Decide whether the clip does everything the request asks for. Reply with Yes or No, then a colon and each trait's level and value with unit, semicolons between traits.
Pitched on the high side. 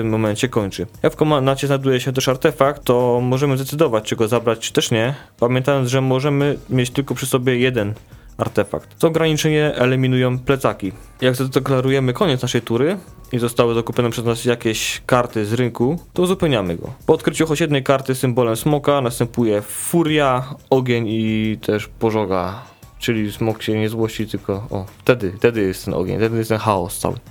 No: low, 120 Hz